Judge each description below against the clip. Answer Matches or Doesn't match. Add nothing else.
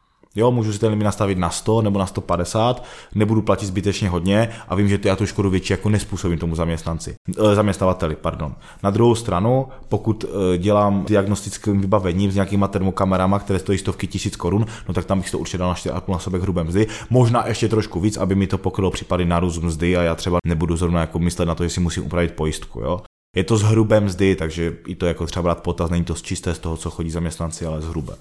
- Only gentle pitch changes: Doesn't match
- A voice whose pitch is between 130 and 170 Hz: Doesn't match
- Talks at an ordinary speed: Doesn't match